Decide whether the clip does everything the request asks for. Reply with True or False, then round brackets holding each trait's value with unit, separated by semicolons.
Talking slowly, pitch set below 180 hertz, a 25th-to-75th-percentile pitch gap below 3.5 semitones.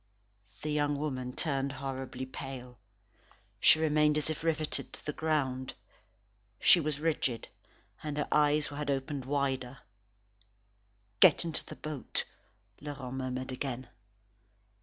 True (120 wpm; 140 Hz; 2.5 semitones)